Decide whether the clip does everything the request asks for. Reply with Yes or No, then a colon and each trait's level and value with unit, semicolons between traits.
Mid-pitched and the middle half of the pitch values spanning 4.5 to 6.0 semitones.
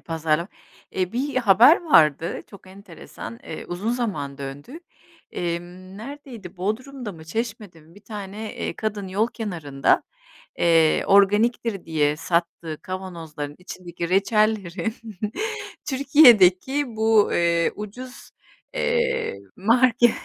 No: high, 195 Hz; average, 5.3 semitones